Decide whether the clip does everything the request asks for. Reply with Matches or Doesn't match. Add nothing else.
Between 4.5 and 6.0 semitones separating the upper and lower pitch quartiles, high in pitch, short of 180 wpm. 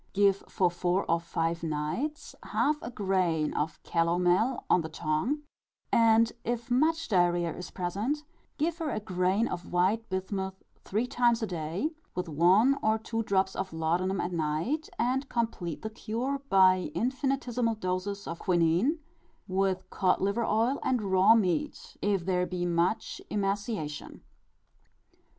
Matches